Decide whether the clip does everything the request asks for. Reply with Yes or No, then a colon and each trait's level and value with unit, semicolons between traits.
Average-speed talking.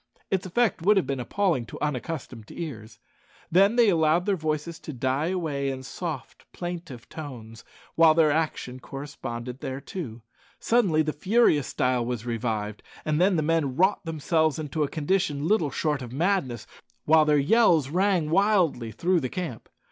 Yes: average, 155 wpm